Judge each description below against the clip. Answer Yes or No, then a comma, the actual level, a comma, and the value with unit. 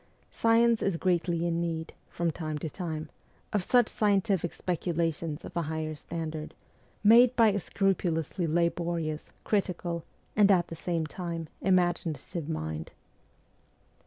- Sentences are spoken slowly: Yes, slow, 130 wpm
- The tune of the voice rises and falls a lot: No, average, 3.0 semitones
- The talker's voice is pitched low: No, medium, 170 Hz